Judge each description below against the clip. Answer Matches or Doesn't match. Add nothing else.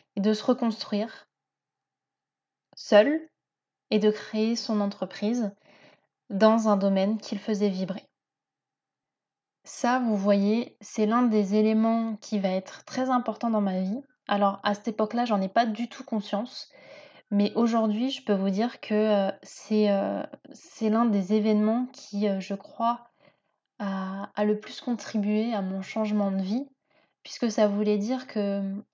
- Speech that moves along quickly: Doesn't match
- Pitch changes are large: Doesn't match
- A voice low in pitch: Doesn't match